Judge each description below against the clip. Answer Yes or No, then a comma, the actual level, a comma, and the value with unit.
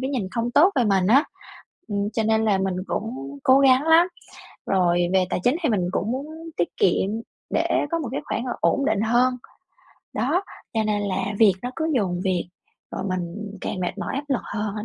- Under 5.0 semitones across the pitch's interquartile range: No, wide, 5.5 semitones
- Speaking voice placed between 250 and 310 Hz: No, high, 215 Hz